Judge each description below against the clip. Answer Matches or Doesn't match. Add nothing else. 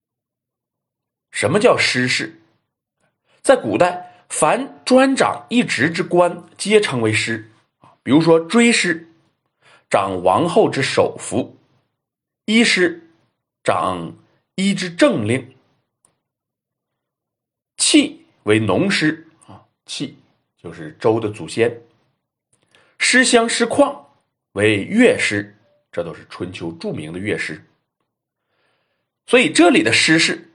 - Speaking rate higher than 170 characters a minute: Doesn't match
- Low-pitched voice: Doesn't match